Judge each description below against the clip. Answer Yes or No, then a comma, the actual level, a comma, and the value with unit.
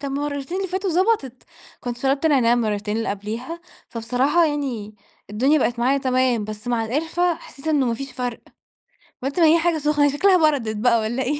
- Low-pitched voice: No, very high, 270 Hz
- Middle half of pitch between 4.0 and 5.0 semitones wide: Yes, average, 4.6 semitones